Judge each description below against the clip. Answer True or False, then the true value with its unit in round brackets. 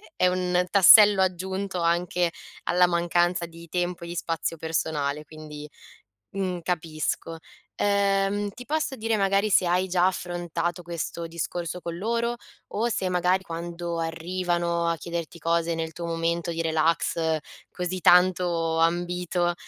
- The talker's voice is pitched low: False (175 Hz)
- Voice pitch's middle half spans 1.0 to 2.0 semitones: True (1.7 semitones)